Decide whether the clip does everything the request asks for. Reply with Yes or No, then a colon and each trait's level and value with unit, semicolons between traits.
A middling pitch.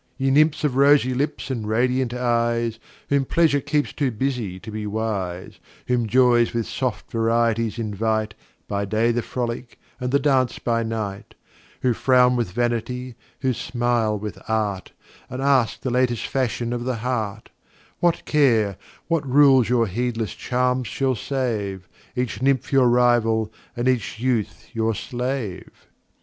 No: low, 120 Hz